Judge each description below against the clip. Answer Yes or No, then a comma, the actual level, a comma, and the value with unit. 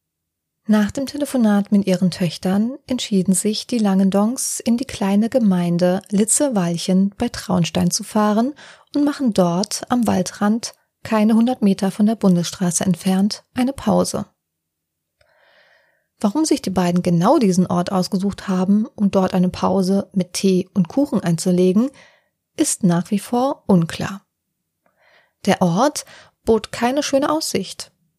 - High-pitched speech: Yes, high, 200 Hz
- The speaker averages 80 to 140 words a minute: Yes, average, 130 wpm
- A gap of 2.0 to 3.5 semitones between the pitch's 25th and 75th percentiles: No, average, 4.7 semitones